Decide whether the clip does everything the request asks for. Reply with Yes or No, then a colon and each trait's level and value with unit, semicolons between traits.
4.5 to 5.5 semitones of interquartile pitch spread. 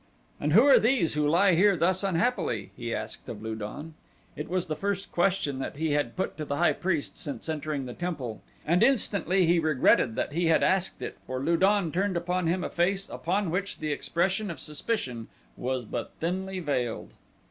Yes: average, 4.8 semitones